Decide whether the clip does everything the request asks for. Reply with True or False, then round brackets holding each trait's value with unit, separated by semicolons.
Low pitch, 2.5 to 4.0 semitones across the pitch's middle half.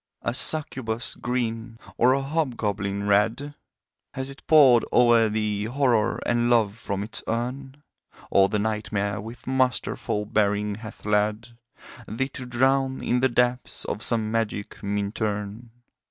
True (115 Hz; 3.3 semitones)